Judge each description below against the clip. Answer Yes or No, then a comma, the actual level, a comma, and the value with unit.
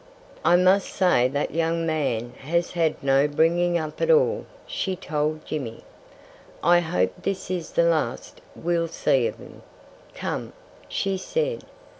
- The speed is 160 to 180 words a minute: No, average, 145 wpm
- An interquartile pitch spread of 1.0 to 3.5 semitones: Yes, average, 3.1 semitones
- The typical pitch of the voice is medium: Yes, medium, 165 Hz